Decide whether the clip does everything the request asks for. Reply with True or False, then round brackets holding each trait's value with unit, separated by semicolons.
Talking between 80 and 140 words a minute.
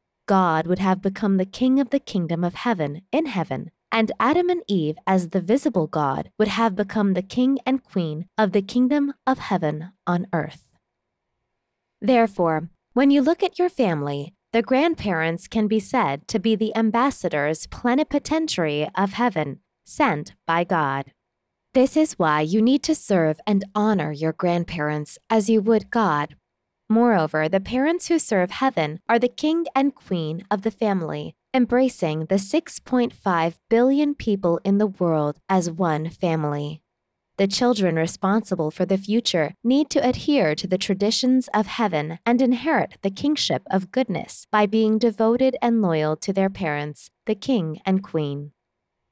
False (160 wpm)